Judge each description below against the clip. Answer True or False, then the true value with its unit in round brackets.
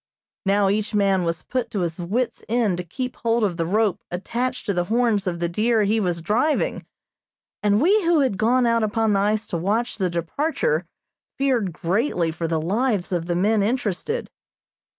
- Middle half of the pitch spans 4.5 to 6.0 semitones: True (5.0 semitones)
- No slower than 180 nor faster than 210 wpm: True (190 wpm)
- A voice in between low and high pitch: False (210 Hz)